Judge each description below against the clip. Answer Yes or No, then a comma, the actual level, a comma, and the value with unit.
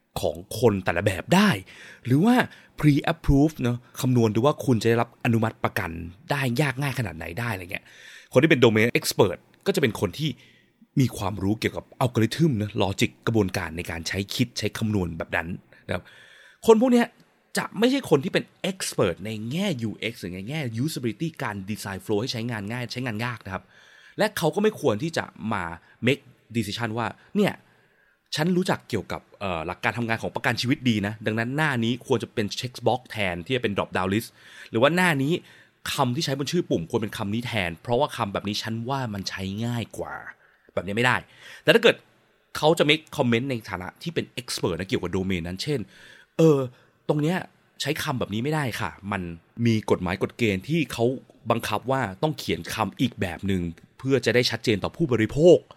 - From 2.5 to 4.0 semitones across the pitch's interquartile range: No, average, 5.1 semitones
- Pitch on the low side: Yes, low, 115 Hz